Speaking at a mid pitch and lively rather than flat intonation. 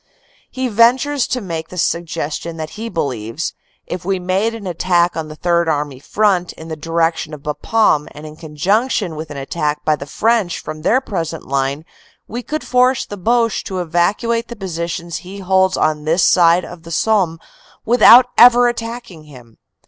Yes: medium, 175 Hz; wide, 5.9 semitones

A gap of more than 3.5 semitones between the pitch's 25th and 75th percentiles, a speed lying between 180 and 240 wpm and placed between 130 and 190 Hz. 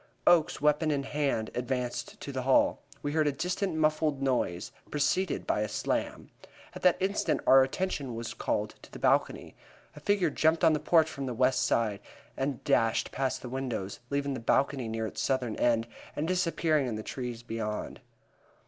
Yes: average, 4.2 semitones; average, 185 wpm; low, 135 Hz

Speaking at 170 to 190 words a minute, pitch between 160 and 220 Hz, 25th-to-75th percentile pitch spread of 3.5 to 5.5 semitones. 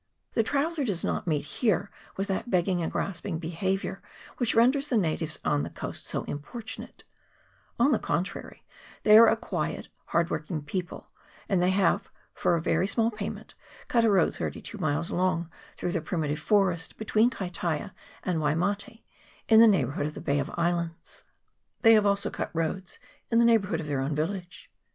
Yes: average, 180 wpm; medium, 185 Hz; average, 4.9 semitones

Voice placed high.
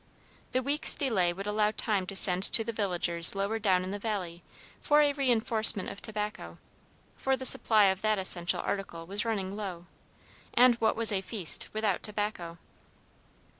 Yes: high, 205 Hz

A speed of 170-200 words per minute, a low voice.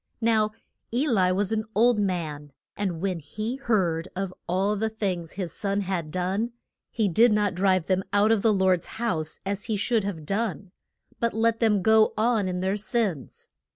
No: average, 185 wpm; high, 200 Hz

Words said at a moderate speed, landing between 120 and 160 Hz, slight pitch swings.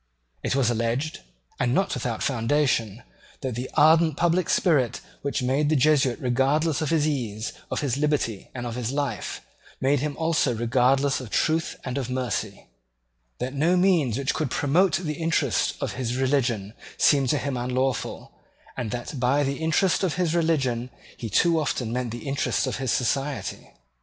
No: average, 170 wpm; low, 135 Hz; average, 3.7 semitones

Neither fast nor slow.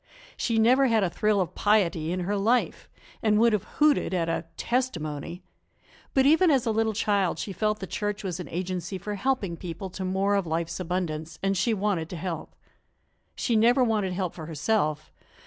Yes: average, 190 wpm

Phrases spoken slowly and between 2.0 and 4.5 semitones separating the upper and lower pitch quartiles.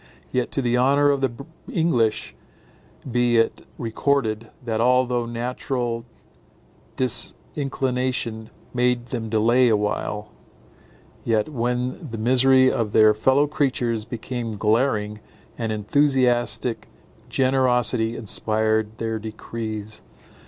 Yes: slow, 100 wpm; narrow, 2.6 semitones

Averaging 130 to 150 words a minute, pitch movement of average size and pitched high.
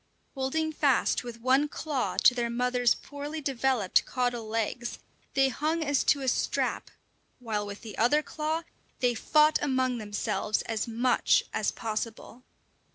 Yes: average, 145 wpm; average, 3.8 semitones; very high, 250 Hz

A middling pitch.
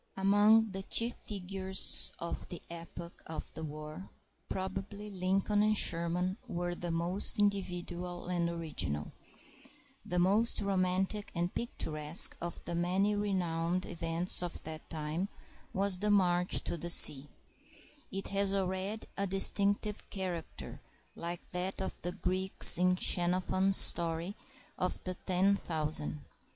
Yes: medium, 180 Hz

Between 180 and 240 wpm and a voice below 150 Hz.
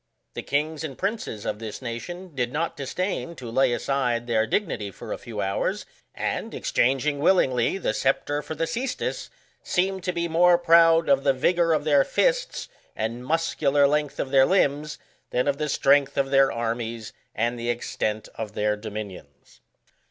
No: average, 170 wpm; medium, 140 Hz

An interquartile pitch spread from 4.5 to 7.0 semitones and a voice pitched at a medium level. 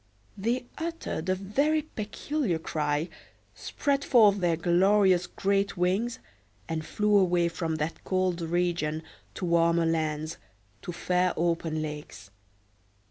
No: average, 3.8 semitones; medium, 180 Hz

